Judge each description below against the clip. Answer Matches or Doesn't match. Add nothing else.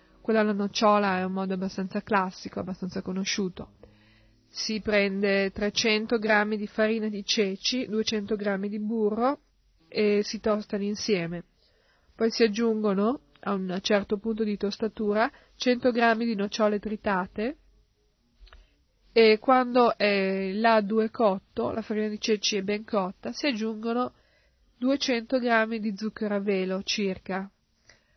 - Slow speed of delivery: Doesn't match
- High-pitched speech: Matches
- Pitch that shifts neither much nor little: Doesn't match